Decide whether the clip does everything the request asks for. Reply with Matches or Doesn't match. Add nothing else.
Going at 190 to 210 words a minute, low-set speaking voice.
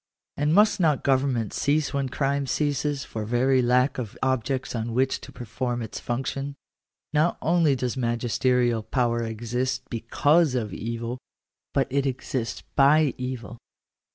Doesn't match